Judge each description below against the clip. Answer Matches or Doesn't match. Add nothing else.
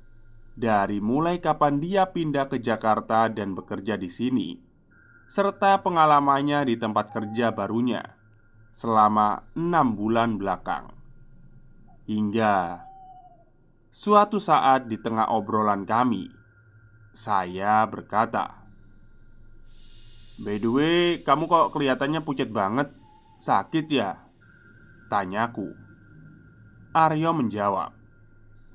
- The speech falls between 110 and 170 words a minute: Doesn't match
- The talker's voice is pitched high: Doesn't match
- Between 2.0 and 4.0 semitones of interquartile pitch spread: Doesn't match